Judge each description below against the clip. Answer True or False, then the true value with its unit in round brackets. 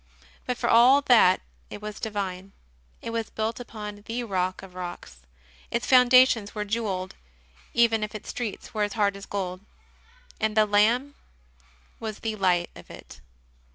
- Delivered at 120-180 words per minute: True (155 wpm)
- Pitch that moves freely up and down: False (2.9 semitones)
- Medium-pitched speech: False (215 Hz)